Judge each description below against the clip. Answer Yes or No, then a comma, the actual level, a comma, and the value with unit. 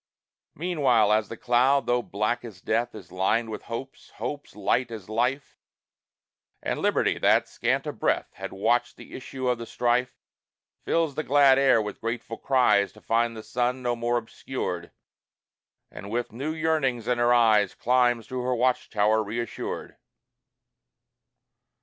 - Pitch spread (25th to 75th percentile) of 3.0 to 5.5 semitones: No, narrow, 2.6 semitones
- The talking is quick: No, average, 150 wpm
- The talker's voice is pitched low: Yes, low, 120 Hz